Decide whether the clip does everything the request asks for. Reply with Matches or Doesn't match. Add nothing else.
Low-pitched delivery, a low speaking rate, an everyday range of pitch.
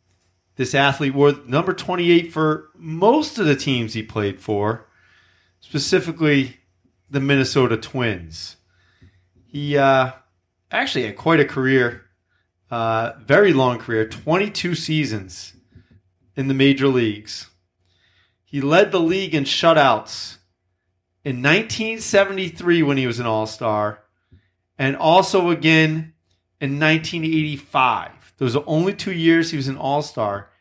Doesn't match